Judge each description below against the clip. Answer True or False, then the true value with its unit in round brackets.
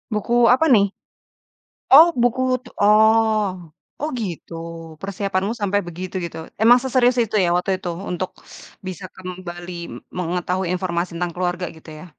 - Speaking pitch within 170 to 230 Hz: True (190 Hz)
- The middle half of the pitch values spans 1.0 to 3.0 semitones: False (3.6 semitones)